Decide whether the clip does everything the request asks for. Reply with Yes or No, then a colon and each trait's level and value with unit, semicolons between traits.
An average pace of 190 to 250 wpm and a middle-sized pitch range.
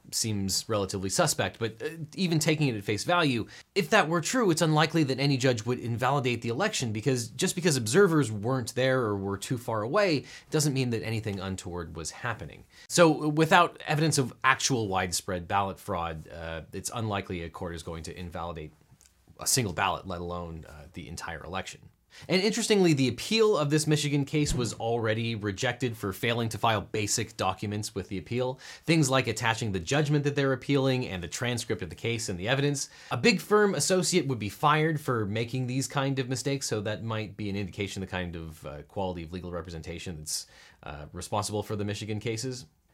No: average, 195 wpm; wide, 6.5 semitones